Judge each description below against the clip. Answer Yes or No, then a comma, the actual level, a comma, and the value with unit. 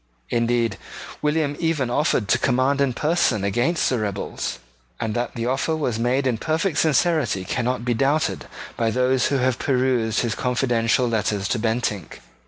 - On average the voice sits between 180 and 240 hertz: No, low, 125 Hz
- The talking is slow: No, average, 160 wpm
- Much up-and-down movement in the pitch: No, average, 3.3 semitones